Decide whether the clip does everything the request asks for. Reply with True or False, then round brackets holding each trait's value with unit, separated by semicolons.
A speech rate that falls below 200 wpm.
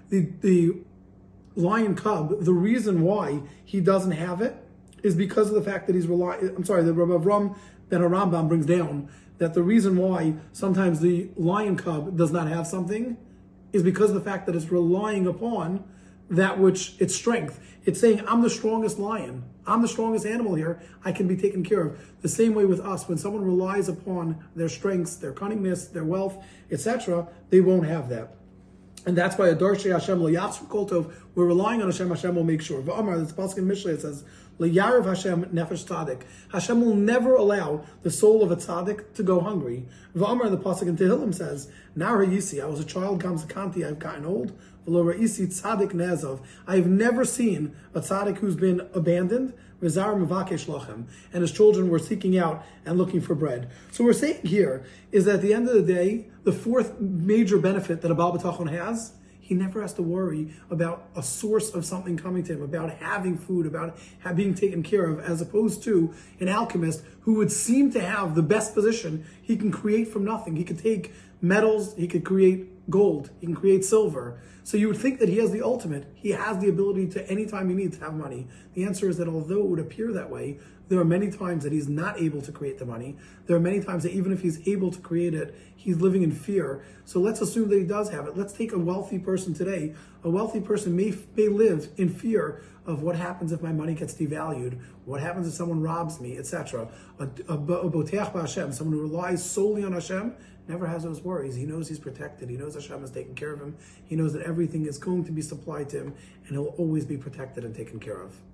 False (205 wpm)